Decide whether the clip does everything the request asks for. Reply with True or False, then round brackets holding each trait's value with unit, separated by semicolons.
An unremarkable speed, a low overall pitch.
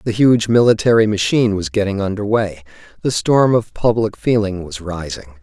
True (165 wpm; 105 Hz)